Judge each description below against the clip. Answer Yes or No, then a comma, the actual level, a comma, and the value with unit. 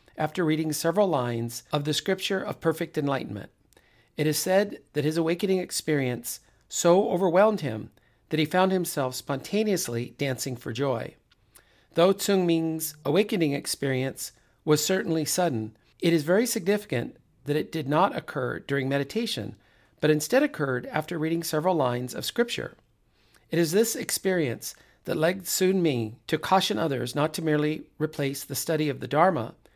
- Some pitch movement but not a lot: No, wide, 5.9 semitones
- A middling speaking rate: Yes, average, 155 wpm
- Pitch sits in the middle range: Yes, medium, 155 Hz